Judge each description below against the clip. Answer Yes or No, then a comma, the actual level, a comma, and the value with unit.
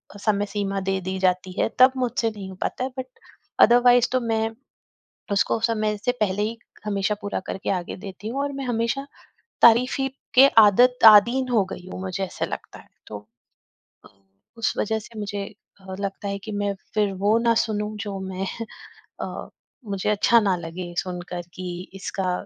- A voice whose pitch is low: No, high, 205 Hz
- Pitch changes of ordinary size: Yes, average, 3.1 semitones